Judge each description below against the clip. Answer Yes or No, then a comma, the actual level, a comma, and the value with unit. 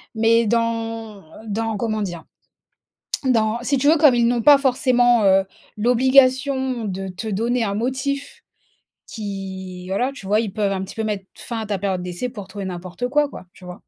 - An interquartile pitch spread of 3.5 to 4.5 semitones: Yes, average, 4.2 semitones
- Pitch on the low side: No, high, 225 Hz